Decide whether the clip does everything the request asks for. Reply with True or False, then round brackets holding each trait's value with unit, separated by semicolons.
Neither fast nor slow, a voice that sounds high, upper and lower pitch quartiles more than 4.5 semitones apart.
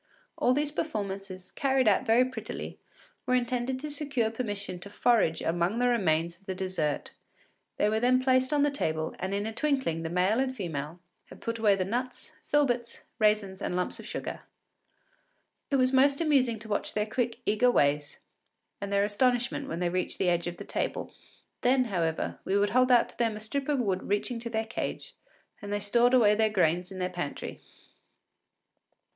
True (190 wpm; 220 Hz; 5.2 semitones)